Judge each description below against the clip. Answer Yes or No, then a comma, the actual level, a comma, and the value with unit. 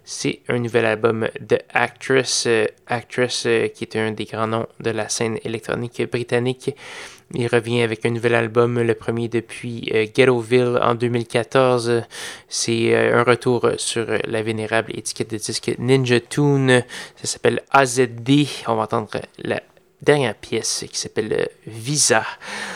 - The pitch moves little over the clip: Yes, narrow, 1.7 semitones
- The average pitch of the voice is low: Yes, low, 120 Hz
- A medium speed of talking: Yes, average, 155 wpm